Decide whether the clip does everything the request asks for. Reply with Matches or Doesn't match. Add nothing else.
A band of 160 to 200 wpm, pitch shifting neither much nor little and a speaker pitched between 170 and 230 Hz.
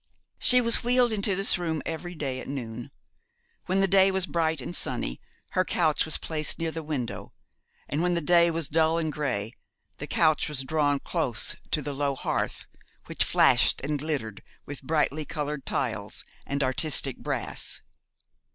Doesn't match